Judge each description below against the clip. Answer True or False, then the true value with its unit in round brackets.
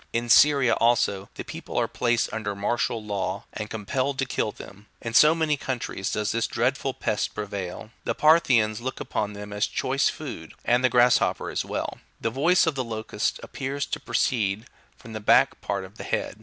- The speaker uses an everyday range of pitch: True (4.1 semitones)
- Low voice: True (115 Hz)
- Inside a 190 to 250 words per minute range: True (195 wpm)